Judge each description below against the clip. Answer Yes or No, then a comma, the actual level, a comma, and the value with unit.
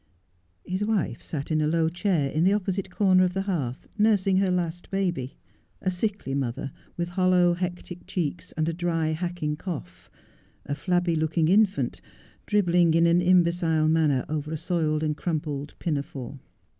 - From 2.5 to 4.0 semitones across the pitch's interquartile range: Yes, average, 2.9 semitones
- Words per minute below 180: Yes, average, 160 wpm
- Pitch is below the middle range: No, medium, 170 Hz